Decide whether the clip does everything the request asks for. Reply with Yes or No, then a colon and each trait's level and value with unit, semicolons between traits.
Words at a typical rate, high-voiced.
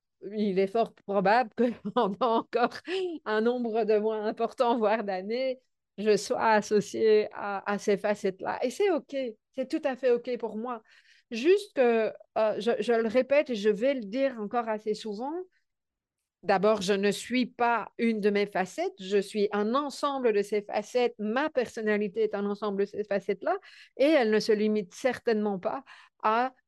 Yes: average, 175 wpm; high, 225 Hz